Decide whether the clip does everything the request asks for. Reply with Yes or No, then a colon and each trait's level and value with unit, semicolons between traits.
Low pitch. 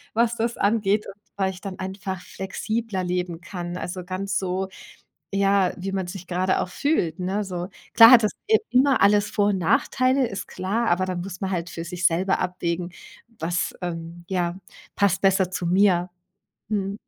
No: high, 190 Hz